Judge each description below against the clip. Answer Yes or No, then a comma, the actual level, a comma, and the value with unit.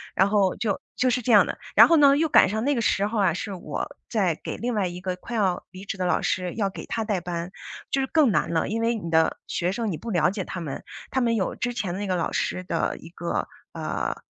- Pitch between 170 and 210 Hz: Yes, high, 200 Hz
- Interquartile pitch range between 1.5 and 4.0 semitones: No, average, 4.4 semitones